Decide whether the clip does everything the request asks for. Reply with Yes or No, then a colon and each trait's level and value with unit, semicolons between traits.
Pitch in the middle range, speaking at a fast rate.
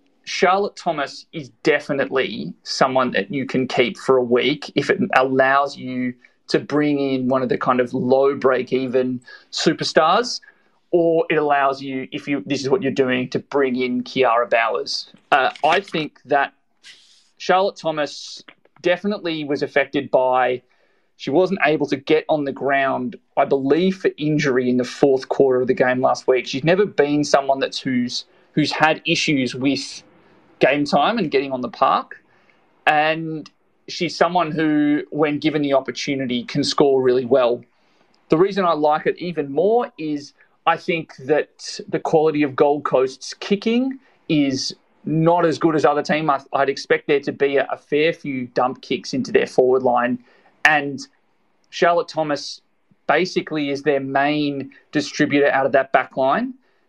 No: medium, 145 Hz; average, 165 wpm